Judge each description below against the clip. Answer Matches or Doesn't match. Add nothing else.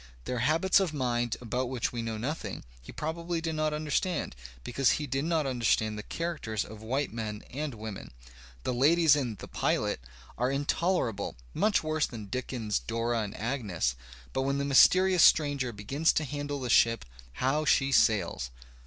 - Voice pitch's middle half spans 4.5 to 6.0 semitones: Matches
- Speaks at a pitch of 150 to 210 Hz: Doesn't match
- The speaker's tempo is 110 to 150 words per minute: Doesn't match